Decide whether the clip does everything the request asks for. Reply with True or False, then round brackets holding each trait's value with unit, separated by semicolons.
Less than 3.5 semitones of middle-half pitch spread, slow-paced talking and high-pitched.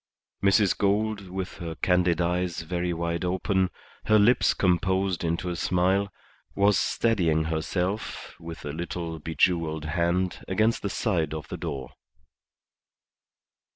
False (2.8 semitones; 125 wpm; 90 Hz)